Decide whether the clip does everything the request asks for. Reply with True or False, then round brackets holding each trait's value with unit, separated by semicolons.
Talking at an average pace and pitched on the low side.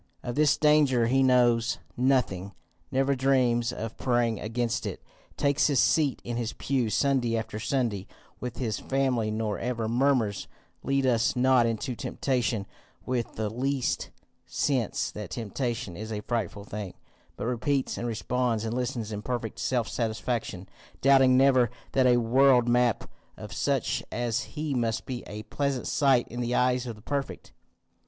True (160 wpm; 120 Hz)